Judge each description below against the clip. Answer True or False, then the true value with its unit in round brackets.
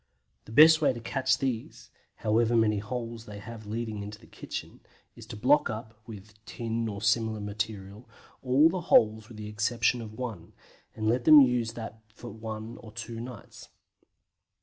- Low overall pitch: True (115 Hz)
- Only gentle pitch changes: True (2.0 semitones)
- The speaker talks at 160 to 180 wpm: True (170 wpm)